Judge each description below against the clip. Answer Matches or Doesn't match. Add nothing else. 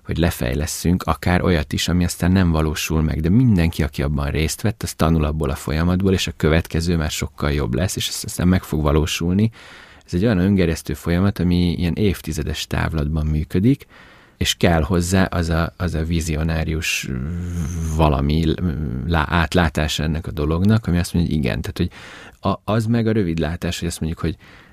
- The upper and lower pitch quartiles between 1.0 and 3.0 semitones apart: Matches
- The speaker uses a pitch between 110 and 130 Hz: Doesn't match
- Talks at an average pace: Doesn't match